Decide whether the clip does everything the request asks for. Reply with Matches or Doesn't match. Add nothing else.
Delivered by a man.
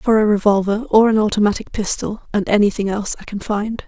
Doesn't match